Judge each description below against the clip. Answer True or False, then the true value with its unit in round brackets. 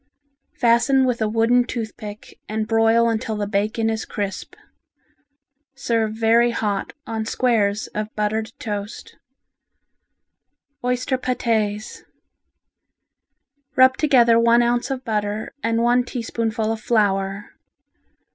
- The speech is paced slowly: True (110 wpm)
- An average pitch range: False (2.0 semitones)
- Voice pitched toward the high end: True (225 Hz)